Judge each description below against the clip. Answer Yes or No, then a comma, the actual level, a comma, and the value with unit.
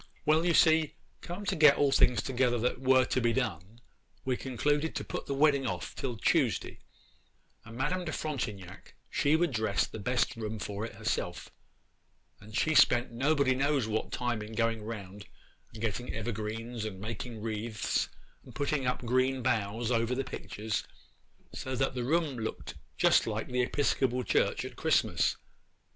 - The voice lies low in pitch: Yes, low, 125 Hz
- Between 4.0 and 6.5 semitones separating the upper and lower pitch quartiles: No, average, 3.6 semitones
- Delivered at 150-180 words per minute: Yes, average, 165 wpm